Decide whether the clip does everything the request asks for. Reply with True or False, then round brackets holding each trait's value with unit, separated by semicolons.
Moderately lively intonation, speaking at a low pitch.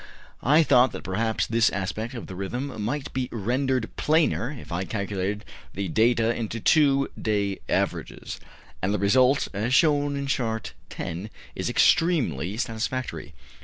True (4.7 semitones; 115 Hz)